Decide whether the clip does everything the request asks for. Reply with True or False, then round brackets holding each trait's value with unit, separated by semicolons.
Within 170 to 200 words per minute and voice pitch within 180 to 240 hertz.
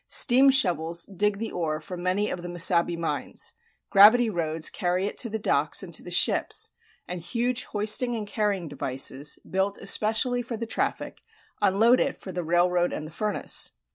True (175 wpm; 190 Hz)